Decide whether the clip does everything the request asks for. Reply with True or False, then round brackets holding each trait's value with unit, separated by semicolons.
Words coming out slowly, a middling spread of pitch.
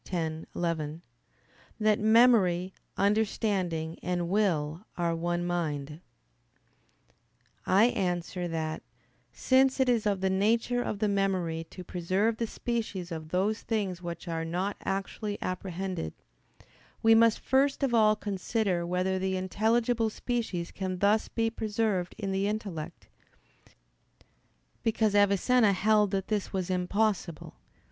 True (125 wpm; 3.8 semitones)